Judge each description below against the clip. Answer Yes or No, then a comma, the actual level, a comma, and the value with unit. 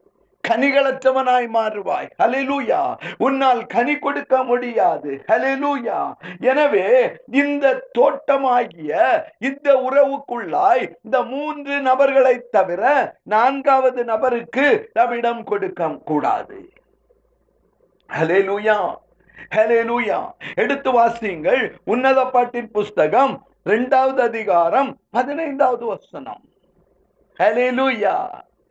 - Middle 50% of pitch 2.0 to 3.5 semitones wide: Yes, average, 3.2 semitones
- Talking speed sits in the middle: No, slow, 70 wpm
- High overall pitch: Yes, very high, 255 Hz